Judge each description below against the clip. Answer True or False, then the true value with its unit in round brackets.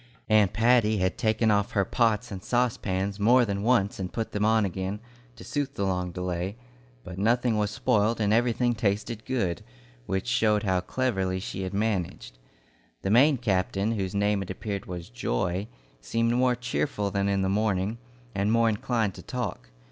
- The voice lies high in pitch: False (105 Hz)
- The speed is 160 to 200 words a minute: True (175 wpm)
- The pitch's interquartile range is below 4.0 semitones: True (3.3 semitones)